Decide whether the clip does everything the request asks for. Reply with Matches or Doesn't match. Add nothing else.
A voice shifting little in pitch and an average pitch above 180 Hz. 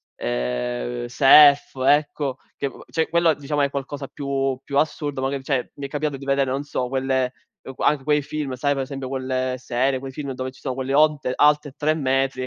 Doesn't match